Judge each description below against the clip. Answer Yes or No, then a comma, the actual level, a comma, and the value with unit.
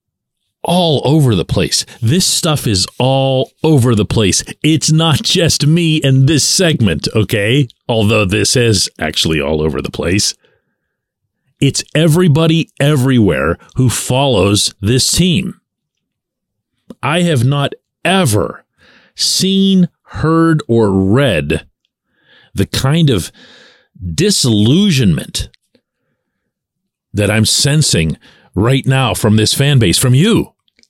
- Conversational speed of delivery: No, slow, 110 wpm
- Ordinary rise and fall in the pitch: No, wide, 6.2 semitones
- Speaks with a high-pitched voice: No, low, 135 Hz